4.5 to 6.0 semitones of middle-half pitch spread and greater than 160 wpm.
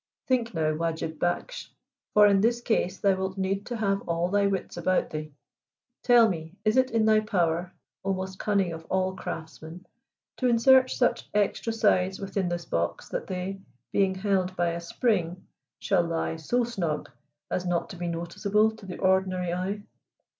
No: average, 3.3 semitones; average, 175 wpm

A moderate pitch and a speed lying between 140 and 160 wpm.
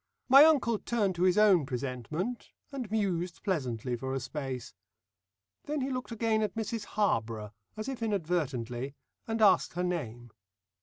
Yes: medium, 180 Hz; average, 150 wpm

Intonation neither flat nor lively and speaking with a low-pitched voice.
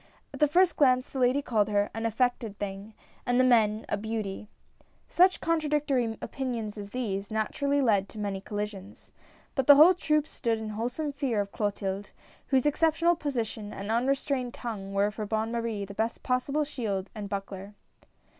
No: average, 4.9 semitones; high, 225 Hz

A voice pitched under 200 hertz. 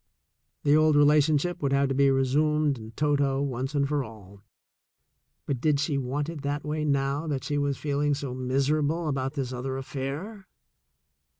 Yes: medium, 140 Hz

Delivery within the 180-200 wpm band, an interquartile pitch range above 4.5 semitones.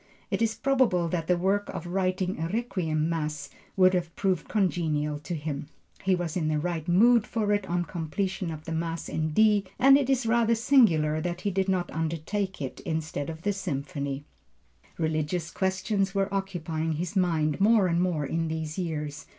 No: average, 185 wpm; average, 3.8 semitones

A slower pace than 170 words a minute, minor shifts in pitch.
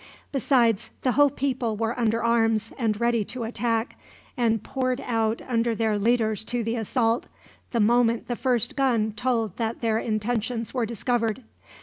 Yes: average, 155 wpm; narrow, 1.6 semitones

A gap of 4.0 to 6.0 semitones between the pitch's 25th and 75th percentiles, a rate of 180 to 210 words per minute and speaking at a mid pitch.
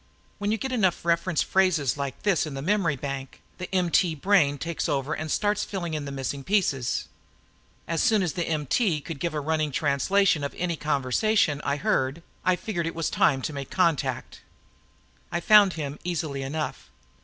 Yes: average, 4.6 semitones; average, 185 wpm; medium, 160 Hz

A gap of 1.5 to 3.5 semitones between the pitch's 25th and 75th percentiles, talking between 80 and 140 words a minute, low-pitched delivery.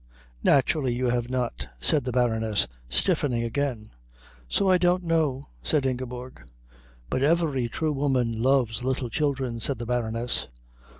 Yes: average, 3.2 semitones; slow, 135 wpm; low, 130 Hz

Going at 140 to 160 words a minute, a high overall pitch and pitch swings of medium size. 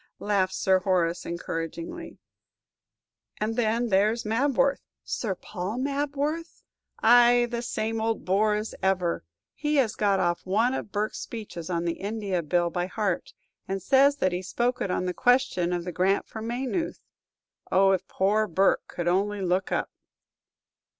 Yes: average, 155 wpm; high, 205 Hz; average, 4.6 semitones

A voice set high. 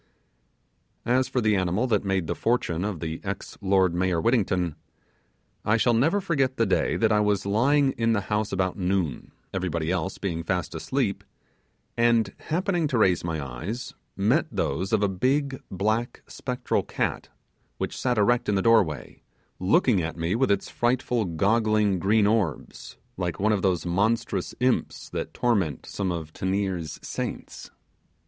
No: low, 100 Hz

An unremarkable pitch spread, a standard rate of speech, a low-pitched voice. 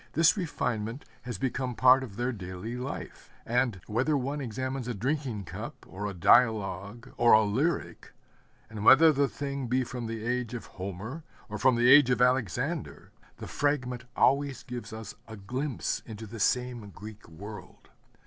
Yes: average, 3.6 semitones; average, 165 wpm; low, 120 Hz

